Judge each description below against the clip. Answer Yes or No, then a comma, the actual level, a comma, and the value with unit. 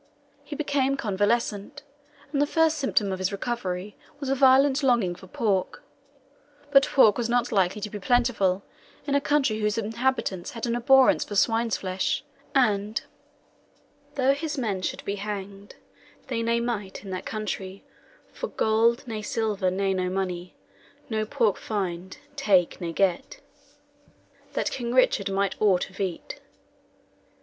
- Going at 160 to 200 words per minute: No, average, 150 wpm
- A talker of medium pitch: No, high, 215 Hz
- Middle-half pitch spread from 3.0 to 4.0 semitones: No, average, 4.6 semitones